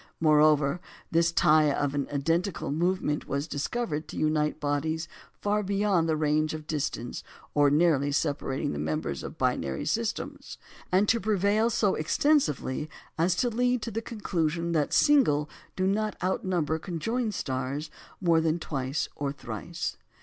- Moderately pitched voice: Yes, medium, 160 Hz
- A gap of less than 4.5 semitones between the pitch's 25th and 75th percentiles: No, average, 4.8 semitones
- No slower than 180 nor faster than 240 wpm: No, average, 140 wpm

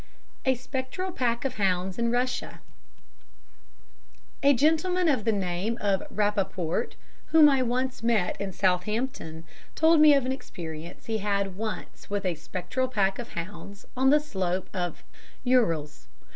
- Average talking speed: Yes, average, 150 wpm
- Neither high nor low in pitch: No, high, 215 Hz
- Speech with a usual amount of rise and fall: No, wide, 5.7 semitones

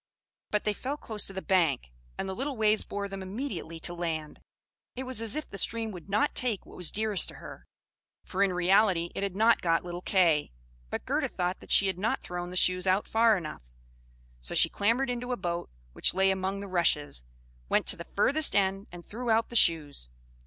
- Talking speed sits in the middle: No, fast, 215 wpm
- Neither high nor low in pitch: No, high, 195 Hz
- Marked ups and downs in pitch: No, average, 3.8 semitones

